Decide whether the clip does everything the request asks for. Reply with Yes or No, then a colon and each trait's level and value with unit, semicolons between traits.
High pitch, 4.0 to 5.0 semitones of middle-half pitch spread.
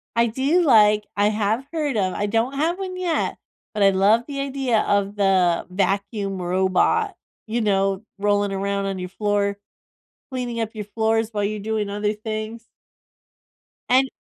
No: high, 210 Hz; average, 2.8 semitones